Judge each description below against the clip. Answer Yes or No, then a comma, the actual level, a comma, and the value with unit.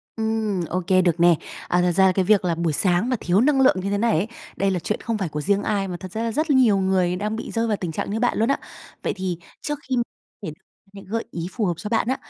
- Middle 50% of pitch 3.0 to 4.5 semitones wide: Yes, average, 3.8 semitones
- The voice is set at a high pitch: Yes, high, 195 Hz